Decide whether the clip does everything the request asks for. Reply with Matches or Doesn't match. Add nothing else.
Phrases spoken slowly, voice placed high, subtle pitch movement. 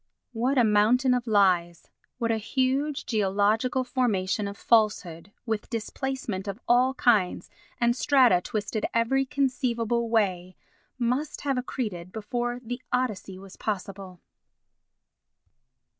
Doesn't match